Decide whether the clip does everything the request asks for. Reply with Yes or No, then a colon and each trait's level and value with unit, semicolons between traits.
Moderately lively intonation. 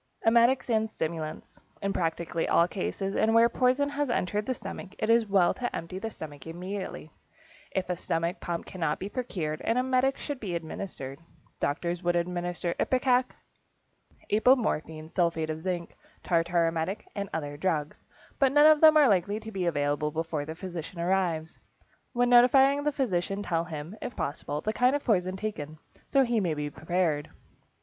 No: wide, 6.0 semitones